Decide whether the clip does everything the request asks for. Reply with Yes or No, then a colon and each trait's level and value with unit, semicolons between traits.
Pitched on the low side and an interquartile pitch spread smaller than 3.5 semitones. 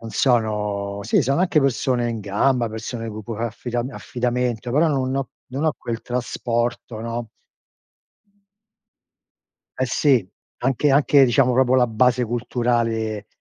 Yes: low, 120 Hz; narrow, 2.4 semitones